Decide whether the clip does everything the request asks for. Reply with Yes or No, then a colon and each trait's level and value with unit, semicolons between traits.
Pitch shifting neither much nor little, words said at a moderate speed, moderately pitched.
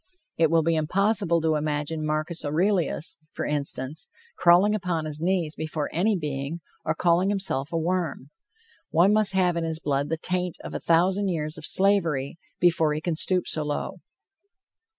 Yes: average, 3.0 semitones; average, 170 wpm; medium, 165 Hz